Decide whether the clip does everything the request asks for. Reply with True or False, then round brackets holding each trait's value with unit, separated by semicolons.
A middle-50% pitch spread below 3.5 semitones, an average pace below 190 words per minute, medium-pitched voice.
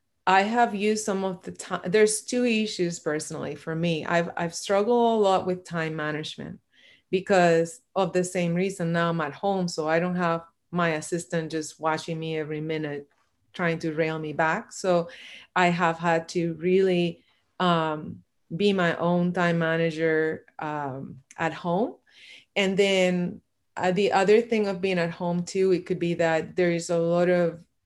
True (2.6 semitones; 175 wpm; 175 Hz)